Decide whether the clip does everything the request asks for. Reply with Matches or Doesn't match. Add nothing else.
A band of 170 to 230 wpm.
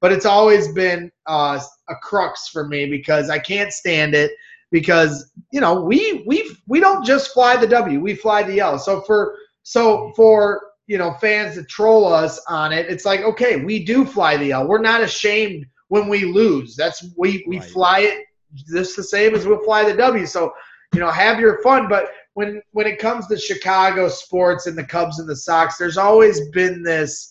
Matches